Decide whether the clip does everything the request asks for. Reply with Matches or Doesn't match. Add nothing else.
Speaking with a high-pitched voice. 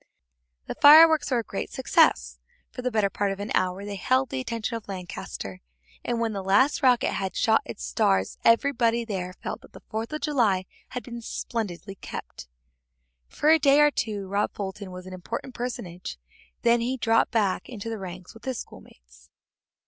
Matches